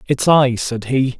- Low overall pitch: Yes, low, 130 Hz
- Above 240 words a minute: No, average, 200 wpm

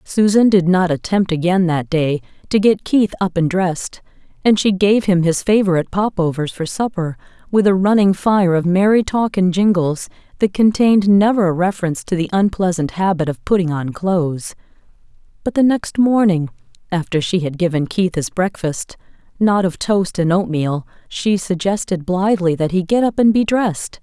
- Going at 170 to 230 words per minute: Yes, average, 175 wpm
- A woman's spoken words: Yes, female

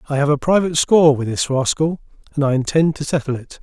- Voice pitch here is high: No, medium, 145 Hz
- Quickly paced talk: Yes, fast, 230 wpm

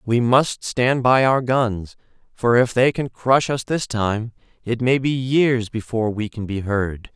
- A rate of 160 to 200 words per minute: Yes, average, 195 wpm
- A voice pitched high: No, low, 120 Hz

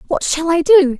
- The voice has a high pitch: Yes, very high, 325 Hz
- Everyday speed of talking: No, fast, 240 wpm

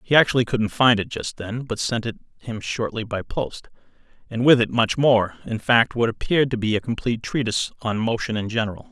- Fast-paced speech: Yes, fast, 210 wpm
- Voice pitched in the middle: No, low, 115 Hz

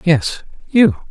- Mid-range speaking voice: Yes, medium, 160 Hz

